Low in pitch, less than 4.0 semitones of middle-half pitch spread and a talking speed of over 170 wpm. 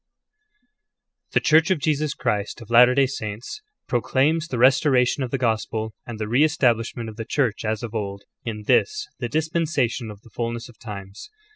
No: low, 120 Hz; average, 4.3 semitones; average, 180 wpm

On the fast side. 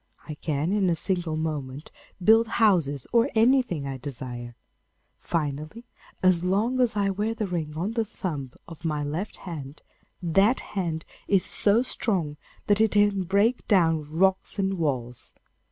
No: average, 155 wpm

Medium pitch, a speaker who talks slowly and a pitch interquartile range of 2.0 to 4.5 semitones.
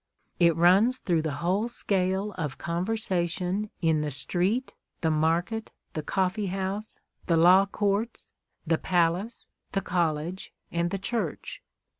Yes: medium, 180 Hz; slow, 130 wpm; average, 3.2 semitones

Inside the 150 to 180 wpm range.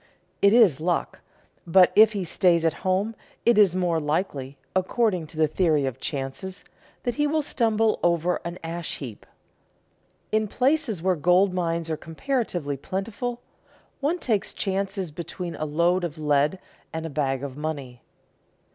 Yes: average, 155 wpm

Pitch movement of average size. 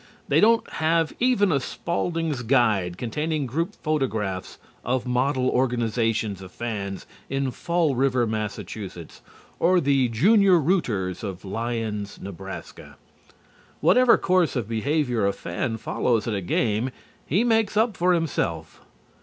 No: wide, 7.2 semitones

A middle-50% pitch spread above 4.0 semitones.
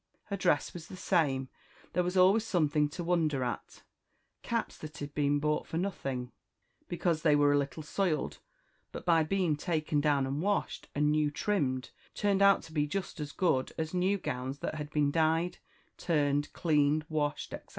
No: average, 3.4 semitones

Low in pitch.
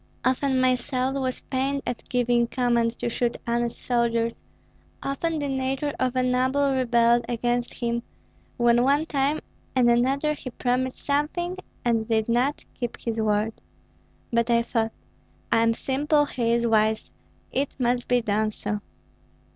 No: high, 245 Hz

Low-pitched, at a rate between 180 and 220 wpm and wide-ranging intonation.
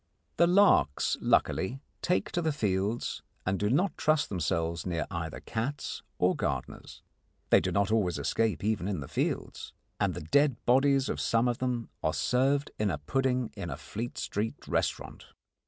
No: low, 110 Hz; average, 170 wpm; wide, 6.8 semitones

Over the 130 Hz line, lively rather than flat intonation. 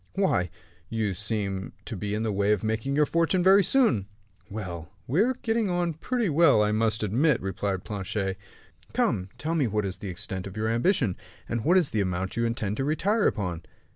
No: low, 110 Hz; wide, 8.7 semitones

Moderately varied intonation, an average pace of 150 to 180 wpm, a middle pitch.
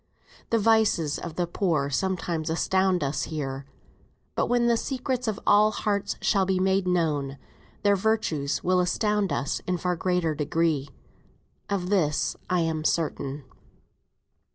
No: average, 4.6 semitones; average, 140 wpm; medium, 180 Hz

